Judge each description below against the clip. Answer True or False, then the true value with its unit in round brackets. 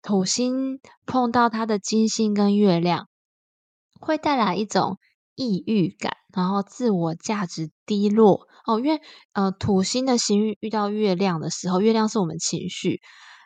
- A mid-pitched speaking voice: False (210 Hz)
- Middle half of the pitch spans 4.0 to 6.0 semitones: False (3.2 semitones)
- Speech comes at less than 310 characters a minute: True (225 characters per minute)